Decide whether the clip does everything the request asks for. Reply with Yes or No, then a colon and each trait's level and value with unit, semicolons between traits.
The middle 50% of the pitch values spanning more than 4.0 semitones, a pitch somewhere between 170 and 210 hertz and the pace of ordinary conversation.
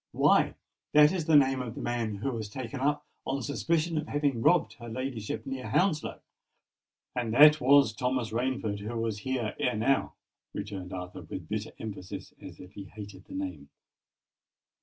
No: average, 4.7 semitones; low, 125 Hz; average, 170 wpm